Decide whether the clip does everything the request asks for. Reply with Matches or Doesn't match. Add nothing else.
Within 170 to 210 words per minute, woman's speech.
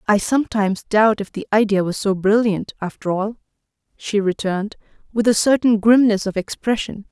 Doesn't match